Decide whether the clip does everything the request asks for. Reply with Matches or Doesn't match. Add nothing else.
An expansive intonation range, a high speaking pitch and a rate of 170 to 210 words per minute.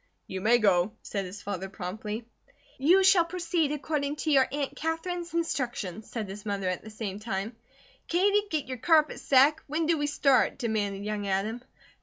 Matches